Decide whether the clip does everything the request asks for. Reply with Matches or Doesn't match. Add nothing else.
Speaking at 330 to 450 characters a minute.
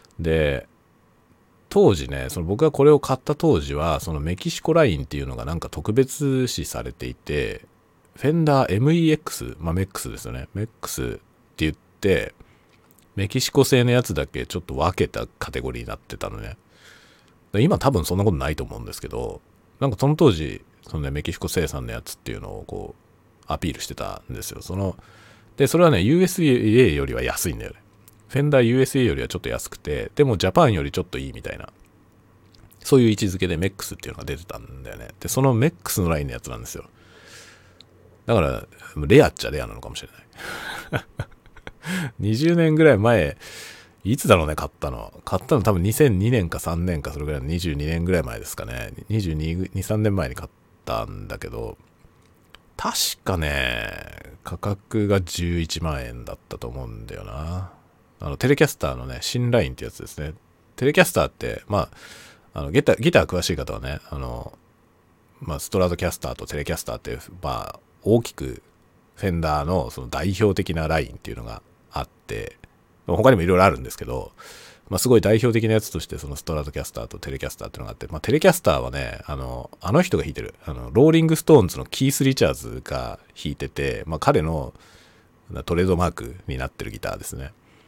Matches